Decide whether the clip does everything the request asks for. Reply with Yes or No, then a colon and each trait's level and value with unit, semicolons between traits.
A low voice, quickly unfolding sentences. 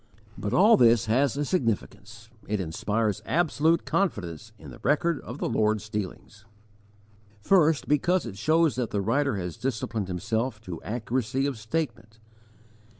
No: low, 115 Hz; average, 145 wpm